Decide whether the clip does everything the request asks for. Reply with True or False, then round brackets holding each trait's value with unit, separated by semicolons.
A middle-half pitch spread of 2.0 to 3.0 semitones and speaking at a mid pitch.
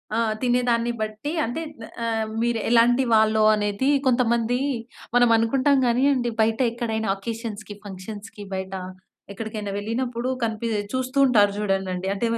False (2.5 semitones; 230 Hz)